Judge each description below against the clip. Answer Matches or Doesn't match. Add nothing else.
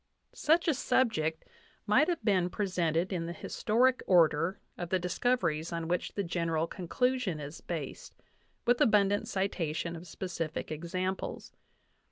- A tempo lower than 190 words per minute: Matches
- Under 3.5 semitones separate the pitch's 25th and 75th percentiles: Doesn't match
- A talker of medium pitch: Matches